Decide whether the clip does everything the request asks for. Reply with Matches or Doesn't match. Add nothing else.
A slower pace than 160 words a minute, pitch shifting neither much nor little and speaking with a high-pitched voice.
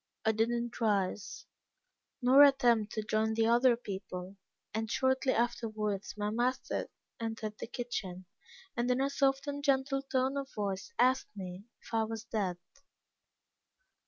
Matches